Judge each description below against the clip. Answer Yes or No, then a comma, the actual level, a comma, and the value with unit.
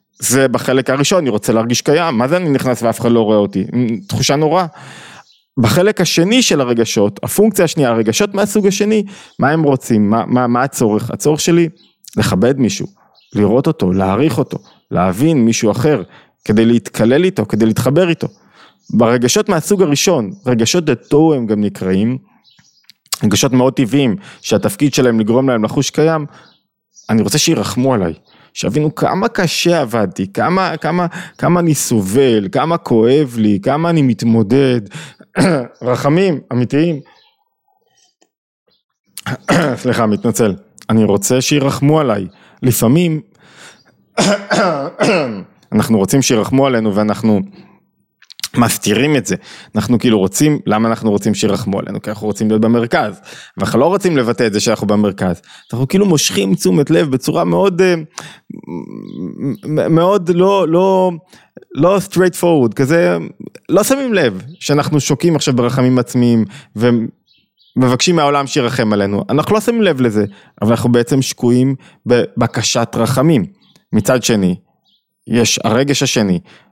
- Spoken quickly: No, average, 130 wpm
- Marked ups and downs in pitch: Yes, wide, 6.6 semitones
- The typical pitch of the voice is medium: No, low, 130 Hz